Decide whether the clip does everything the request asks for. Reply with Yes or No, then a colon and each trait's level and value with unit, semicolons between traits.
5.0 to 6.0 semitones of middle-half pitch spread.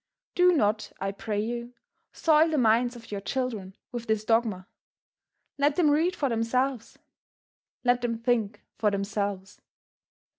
No: average, 3.6 semitones